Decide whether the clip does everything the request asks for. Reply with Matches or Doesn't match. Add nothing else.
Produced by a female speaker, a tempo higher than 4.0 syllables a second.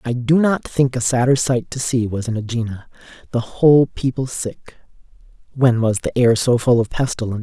Doesn't match